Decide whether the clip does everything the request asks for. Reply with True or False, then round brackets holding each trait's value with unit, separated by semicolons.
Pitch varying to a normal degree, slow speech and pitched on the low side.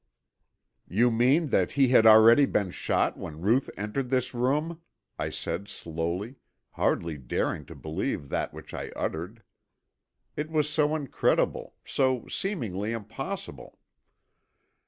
False (6.3 semitones; 125 wpm; 115 Hz)